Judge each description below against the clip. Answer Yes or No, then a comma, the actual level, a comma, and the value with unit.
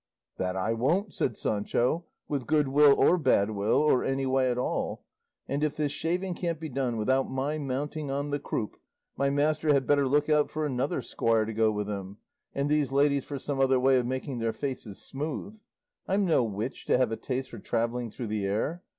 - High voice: No, low, 135 Hz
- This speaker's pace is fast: Yes, fast, 210 wpm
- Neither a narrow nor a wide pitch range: Yes, average, 4.1 semitones